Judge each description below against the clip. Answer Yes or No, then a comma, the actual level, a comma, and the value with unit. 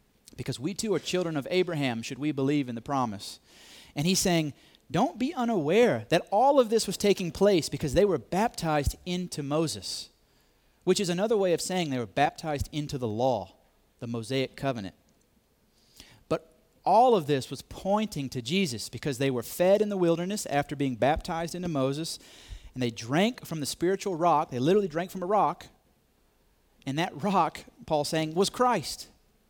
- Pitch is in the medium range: Yes, medium, 155 Hz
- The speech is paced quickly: No, average, 175 wpm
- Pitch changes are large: Yes, wide, 5.8 semitones